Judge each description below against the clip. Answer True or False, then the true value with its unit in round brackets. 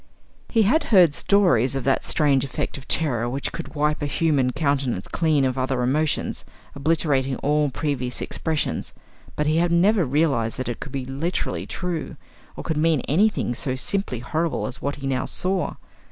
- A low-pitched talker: False (145 Hz)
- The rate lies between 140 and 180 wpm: True (175 wpm)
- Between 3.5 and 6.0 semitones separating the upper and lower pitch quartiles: True (3.9 semitones)